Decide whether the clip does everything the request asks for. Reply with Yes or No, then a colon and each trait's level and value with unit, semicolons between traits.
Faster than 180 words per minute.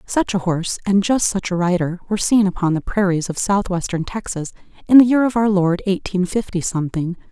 Yes: fast, 205 wpm